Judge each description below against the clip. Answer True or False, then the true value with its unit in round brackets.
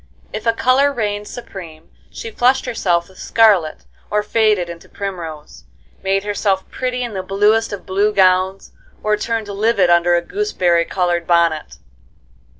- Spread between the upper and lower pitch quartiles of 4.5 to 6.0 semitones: False (4.1 semitones)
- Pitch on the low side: False (200 Hz)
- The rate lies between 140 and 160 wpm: True (150 wpm)